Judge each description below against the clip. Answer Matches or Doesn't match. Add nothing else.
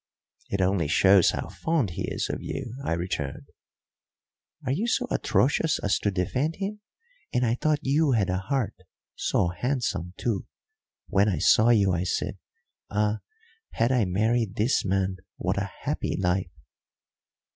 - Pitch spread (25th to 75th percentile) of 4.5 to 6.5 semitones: Matches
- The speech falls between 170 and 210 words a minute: Doesn't match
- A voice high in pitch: Doesn't match